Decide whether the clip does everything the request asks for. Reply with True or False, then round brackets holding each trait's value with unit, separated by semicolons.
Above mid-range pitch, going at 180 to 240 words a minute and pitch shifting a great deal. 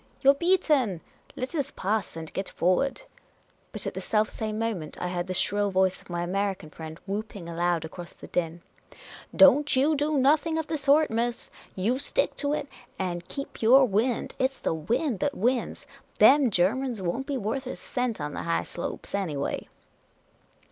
True (220 Hz; 190 wpm; 7.3 semitones)